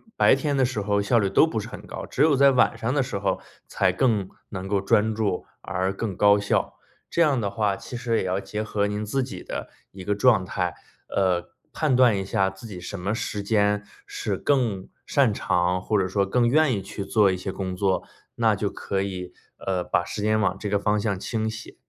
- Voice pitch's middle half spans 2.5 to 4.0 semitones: Yes, average, 3.1 semitones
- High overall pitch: No, low, 105 Hz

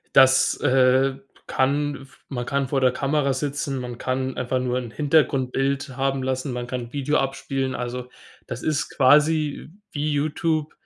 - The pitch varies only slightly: Yes, narrow, 2.0 semitones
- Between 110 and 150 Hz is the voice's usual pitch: Yes, low, 135 Hz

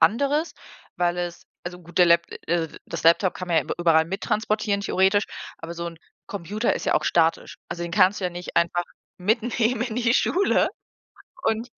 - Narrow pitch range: No, average, 4.2 semitones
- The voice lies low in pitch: No, medium, 185 Hz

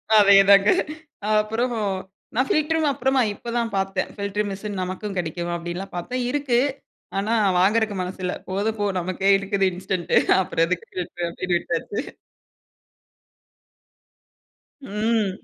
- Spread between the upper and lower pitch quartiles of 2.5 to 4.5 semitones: Yes, average, 3.5 semitones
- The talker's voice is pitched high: Yes, high, 200 Hz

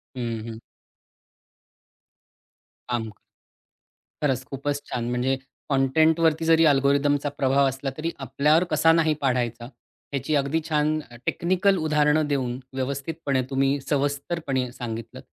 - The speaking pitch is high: No, medium, 140 Hz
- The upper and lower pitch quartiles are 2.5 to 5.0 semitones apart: Yes, average, 3.0 semitones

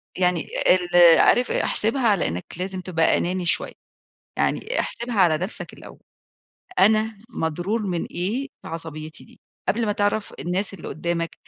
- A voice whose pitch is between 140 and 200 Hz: Yes, medium, 185 Hz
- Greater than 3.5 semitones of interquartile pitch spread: Yes, average, 4.0 semitones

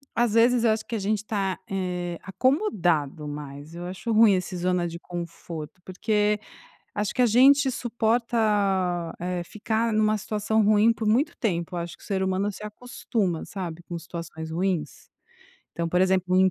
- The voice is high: Yes, high, 195 Hz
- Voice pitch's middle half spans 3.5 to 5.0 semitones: Yes, average, 4.1 semitones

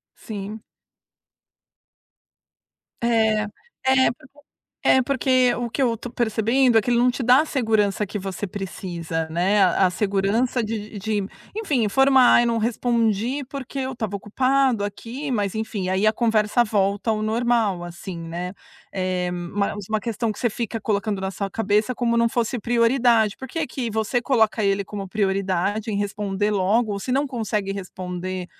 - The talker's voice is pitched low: No, high, 215 Hz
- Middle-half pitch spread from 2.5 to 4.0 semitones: Yes, average, 3.5 semitones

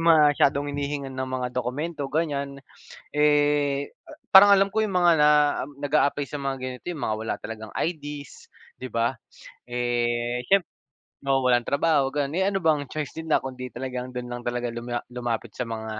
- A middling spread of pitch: Yes, average, 3.3 semitones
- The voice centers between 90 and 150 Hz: Yes, medium, 140 Hz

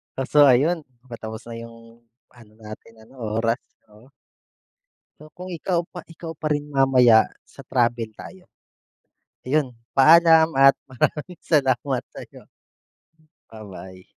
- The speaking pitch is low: Yes, low, 130 Hz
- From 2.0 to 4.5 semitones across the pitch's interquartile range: No, average, 4.9 semitones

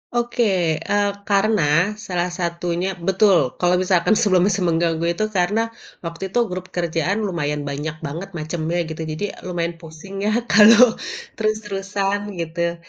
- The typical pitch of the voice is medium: Yes, medium, 180 Hz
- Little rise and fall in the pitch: No, average, 3.3 semitones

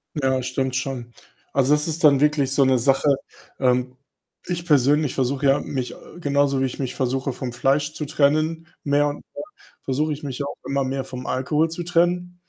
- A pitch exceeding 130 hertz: Yes, medium, 140 Hz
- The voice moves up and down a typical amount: No, narrow, 2.3 semitones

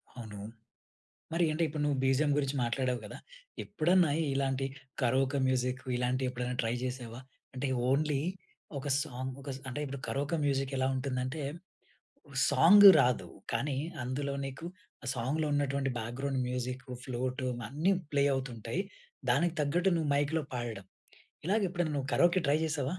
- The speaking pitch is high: No, low, 135 Hz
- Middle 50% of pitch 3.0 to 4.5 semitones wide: No, narrow, 2.6 semitones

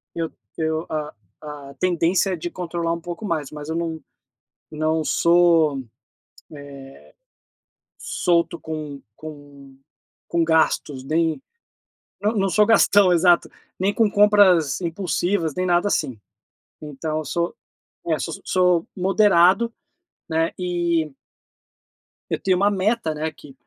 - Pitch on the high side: No, medium, 170 Hz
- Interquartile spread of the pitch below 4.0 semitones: Yes, average, 2.8 semitones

